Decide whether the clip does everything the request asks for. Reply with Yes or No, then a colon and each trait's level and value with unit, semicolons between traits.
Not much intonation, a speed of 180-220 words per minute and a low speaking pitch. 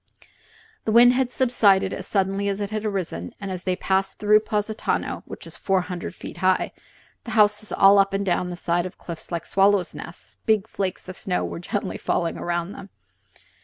No: narrow, 2.3 semitones; average, 200 wpm; high, 195 Hz